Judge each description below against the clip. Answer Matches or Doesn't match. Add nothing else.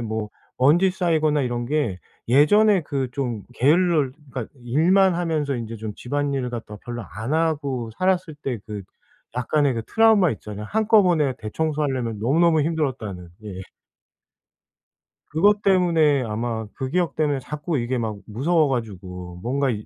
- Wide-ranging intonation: Matches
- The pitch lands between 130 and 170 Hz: Matches